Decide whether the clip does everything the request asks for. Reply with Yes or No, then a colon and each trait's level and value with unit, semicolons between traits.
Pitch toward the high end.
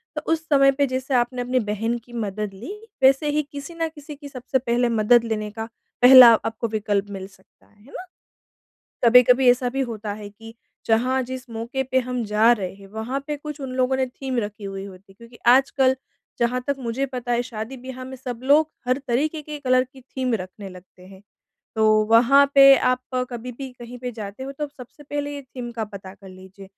Yes: high, 245 Hz